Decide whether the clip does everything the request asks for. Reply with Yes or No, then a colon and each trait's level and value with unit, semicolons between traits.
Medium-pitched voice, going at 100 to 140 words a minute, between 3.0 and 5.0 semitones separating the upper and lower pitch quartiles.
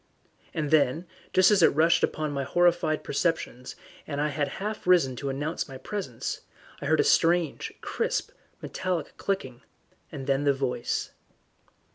No: medium, 155 Hz; average, 150 wpm; average, 4.1 semitones